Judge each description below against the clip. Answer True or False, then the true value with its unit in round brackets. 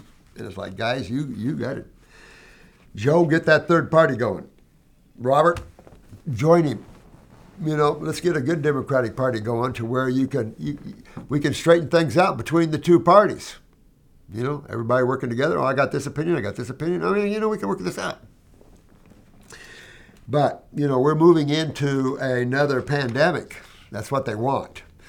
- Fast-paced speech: False (180 wpm)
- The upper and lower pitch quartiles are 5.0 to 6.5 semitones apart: False (4.5 semitones)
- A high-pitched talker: False (140 Hz)